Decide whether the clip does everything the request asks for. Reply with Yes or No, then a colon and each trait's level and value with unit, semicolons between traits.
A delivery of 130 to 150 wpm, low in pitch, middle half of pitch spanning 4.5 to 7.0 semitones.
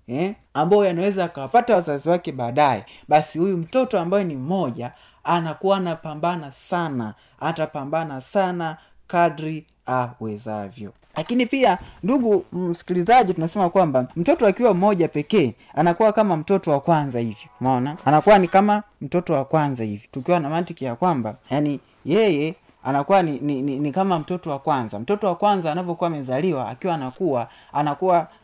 No: fast, 140 wpm; medium, 160 Hz; average, 5.1 semitones